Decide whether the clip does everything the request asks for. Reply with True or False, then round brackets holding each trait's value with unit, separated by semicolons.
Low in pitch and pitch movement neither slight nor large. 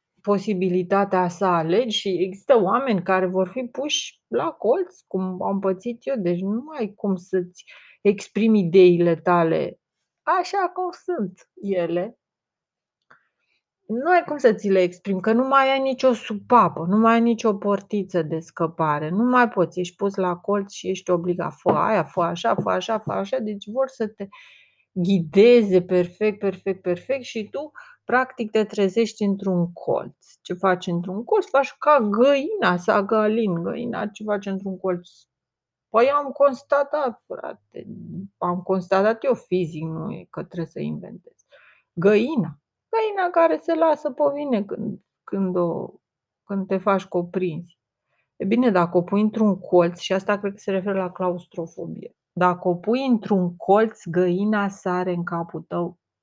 False (200 Hz; 4.4 semitones)